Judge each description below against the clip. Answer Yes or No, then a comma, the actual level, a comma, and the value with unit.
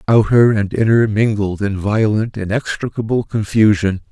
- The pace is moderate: No, slow, 115 wpm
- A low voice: Yes, low, 105 Hz